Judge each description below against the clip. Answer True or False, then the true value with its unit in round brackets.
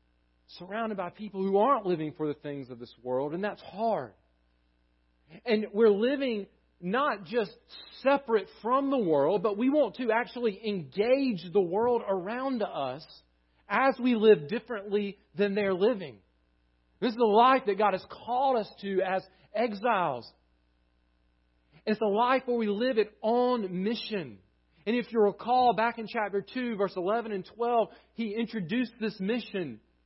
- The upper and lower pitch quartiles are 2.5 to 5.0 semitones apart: False (5.5 semitones)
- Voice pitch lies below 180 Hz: False (210 Hz)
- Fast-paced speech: False (155 wpm)